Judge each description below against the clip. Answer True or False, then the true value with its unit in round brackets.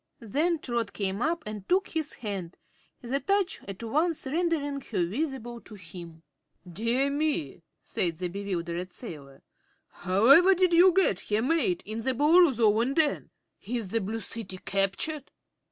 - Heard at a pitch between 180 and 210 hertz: False (235 Hz)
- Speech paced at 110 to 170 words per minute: True (150 wpm)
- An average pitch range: False (8.1 semitones)